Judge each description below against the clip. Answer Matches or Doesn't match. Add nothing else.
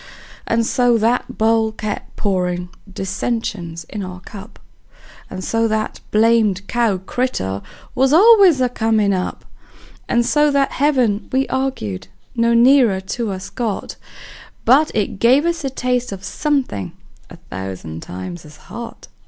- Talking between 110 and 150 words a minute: Matches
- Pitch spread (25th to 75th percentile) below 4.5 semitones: Doesn't match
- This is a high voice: Matches